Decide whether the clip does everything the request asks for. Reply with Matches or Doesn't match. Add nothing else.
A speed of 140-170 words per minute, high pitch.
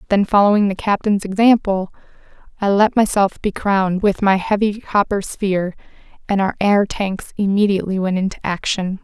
Matches